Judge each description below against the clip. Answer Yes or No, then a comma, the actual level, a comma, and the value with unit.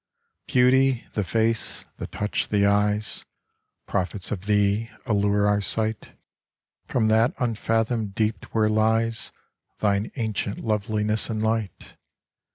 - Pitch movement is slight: Yes, narrow, 1.7 semitones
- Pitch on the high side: No, low, 110 Hz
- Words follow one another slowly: Yes, slow, 115 wpm